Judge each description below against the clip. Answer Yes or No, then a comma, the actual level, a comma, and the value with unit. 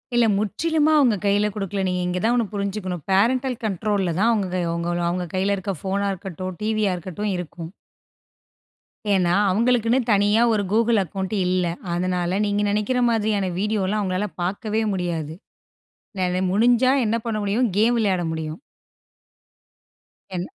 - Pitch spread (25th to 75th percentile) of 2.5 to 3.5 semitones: Yes, average, 3.1 semitones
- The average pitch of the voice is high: Yes, high, 200 Hz